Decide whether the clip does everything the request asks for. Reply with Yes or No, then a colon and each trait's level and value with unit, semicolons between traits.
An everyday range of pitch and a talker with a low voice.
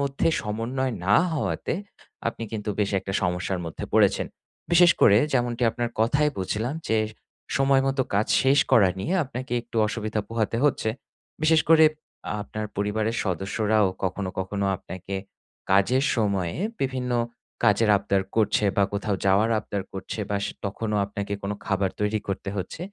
Yes: average, 3.9 semitones; low, 105 Hz